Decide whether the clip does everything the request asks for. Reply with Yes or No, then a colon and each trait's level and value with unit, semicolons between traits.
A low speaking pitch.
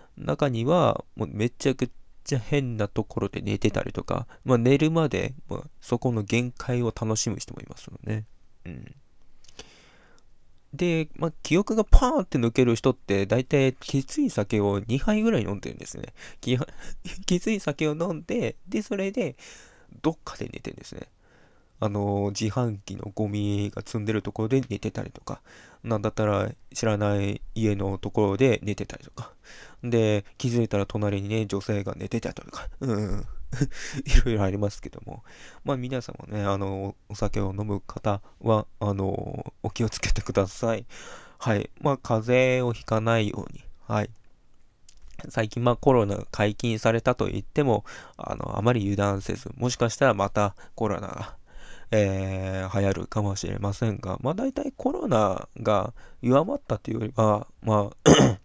Yes: low, 110 Hz